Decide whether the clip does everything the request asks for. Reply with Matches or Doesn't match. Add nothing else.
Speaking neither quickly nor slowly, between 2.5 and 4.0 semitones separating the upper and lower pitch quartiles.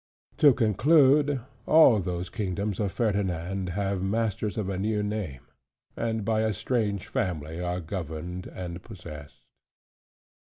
Doesn't match